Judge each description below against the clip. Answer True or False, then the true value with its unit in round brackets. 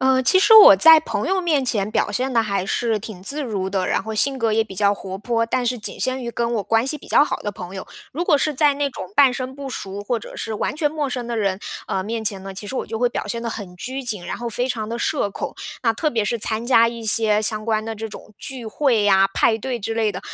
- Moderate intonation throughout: True (3.9 semitones)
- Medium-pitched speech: False (230 Hz)